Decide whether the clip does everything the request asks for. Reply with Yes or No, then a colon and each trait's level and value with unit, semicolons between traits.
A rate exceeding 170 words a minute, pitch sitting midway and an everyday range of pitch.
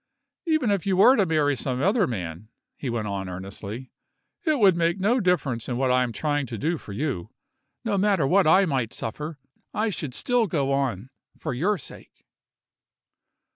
No: average, 180 wpm; medium, 145 Hz; wide, 8.2 semitones